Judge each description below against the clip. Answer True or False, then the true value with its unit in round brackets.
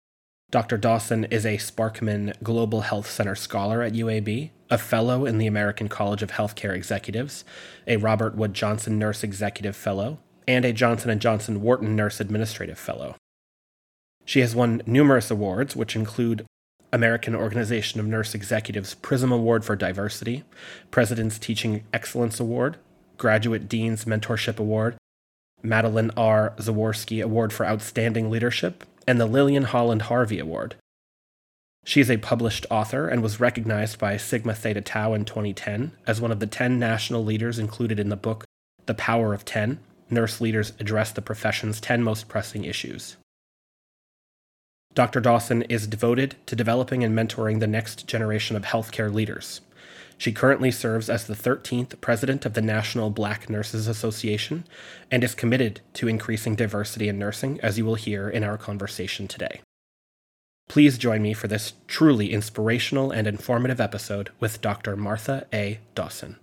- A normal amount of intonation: False (1.9 semitones)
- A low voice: True (110 Hz)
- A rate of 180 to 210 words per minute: False (155 wpm)